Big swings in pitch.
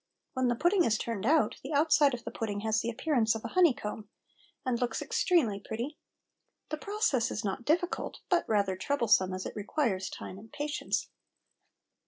Yes: wide, 5.9 semitones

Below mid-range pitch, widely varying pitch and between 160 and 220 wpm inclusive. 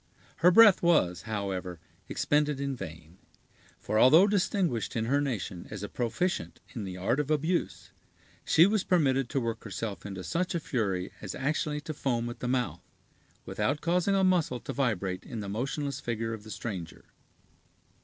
Yes: low, 125 Hz; wide, 7.1 semitones; average, 170 wpm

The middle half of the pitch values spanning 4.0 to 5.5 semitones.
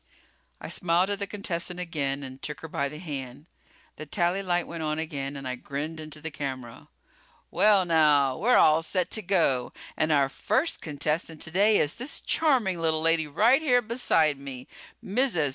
Yes: average, 4.9 semitones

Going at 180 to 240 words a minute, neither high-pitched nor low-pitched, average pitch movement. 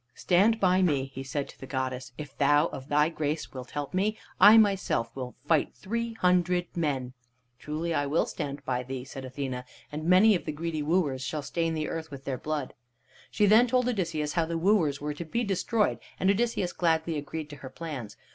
Yes: fast, 205 wpm; medium, 155 Hz; average, 4.8 semitones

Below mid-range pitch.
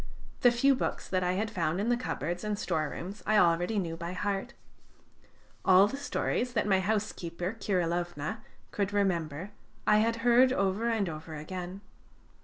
No: high, 195 Hz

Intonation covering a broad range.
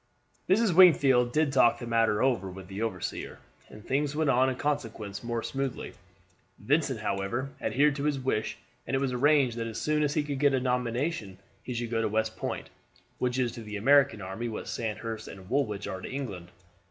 No: average, 4.1 semitones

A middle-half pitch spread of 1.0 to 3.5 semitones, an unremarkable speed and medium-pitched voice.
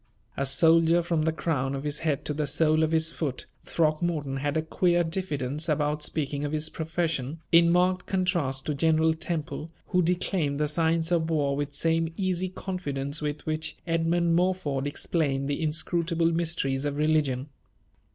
Yes: narrow, 2.5 semitones; average, 165 wpm; medium, 160 Hz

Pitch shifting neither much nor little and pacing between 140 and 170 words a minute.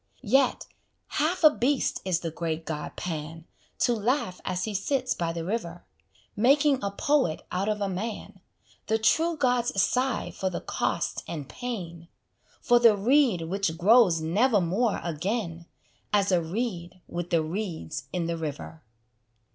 No: wide, 6.2 semitones; average, 150 wpm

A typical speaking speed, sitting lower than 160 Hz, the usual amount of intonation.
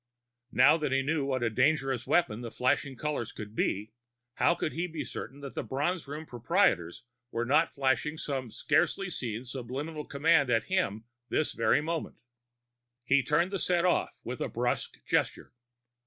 Yes: average, 170 wpm; medium, 140 Hz; average, 4.5 semitones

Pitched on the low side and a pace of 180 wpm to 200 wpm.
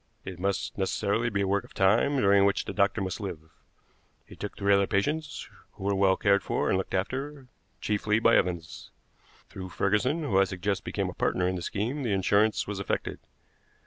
Yes: low, 100 Hz; average, 195 wpm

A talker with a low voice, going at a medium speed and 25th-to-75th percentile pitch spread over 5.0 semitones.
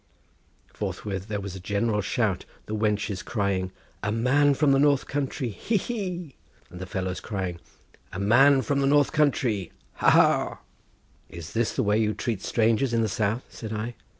Yes: low, 110 Hz; average, 170 wpm; wide, 5.4 semitones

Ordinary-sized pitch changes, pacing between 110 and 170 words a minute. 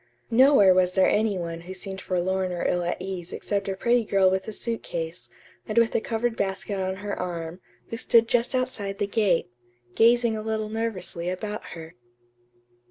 No: average, 3.5 semitones; average, 185 wpm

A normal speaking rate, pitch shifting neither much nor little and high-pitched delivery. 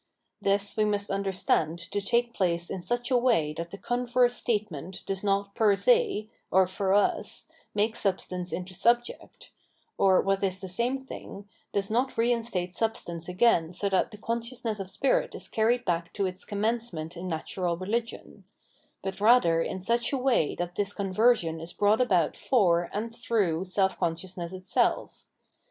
Yes: average, 165 wpm; average, 4.3 semitones; high, 200 Hz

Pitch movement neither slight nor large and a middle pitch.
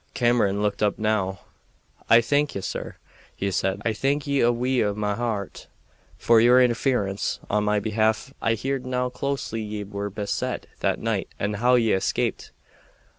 No: average, 3.4 semitones; low, 110 Hz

